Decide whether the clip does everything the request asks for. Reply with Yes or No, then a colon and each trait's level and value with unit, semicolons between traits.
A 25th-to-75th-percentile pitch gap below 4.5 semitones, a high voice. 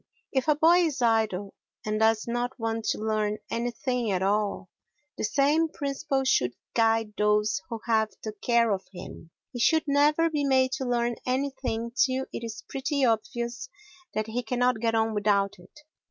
Yes: average, 3.6 semitones; high, 235 Hz